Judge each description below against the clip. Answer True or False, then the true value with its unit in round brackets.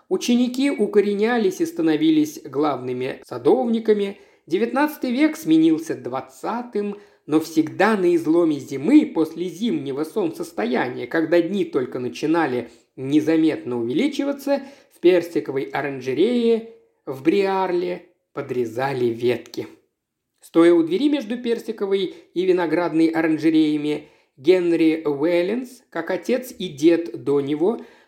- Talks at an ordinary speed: False (100 wpm)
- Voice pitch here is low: False (195 Hz)